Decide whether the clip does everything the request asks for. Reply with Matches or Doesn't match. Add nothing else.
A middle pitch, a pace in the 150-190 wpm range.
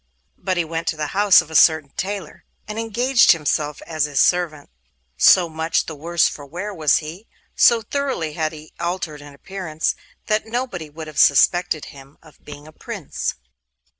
Matches